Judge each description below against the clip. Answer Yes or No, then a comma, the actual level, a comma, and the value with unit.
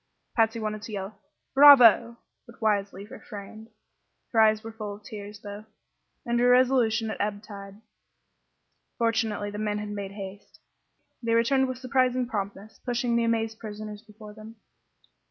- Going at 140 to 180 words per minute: Yes, average, 150 wpm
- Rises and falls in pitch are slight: Yes, narrow, 2.1 semitones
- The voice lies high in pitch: Yes, high, 220 Hz